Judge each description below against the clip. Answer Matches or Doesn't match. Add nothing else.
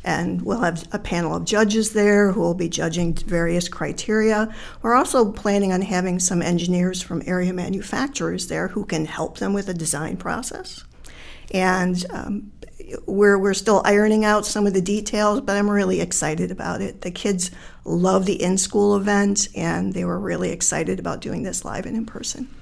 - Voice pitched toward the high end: Matches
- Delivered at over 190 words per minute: Doesn't match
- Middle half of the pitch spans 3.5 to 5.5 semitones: Doesn't match